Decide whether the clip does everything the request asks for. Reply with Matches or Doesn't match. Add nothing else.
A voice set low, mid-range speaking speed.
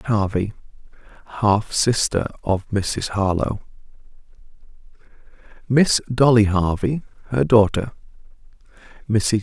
Doesn't match